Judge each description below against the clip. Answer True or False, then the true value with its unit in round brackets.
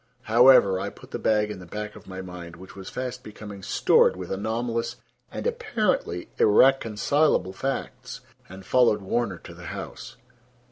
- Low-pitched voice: True (105 Hz)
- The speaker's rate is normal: True (155 wpm)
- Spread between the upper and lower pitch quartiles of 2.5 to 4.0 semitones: False (4.5 semitones)